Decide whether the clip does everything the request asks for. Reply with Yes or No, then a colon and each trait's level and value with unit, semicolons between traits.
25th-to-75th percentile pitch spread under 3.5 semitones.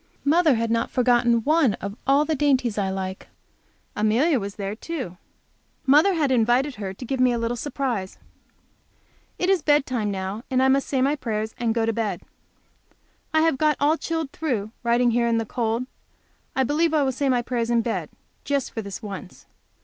No: average, 4.2 semitones